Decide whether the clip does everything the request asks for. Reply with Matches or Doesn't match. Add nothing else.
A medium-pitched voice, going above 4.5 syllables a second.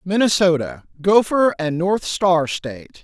Doesn't match